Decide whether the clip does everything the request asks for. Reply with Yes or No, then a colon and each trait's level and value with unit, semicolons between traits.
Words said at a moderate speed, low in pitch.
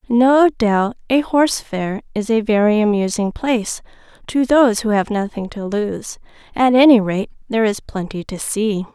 No: average, 170 wpm; high, 220 Hz